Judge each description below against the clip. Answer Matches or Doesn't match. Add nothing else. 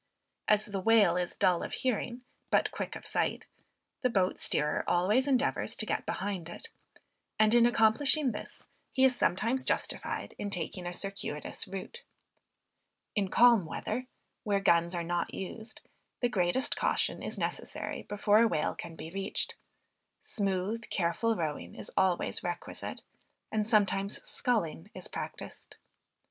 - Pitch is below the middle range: Doesn't match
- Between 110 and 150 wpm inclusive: Matches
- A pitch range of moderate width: Matches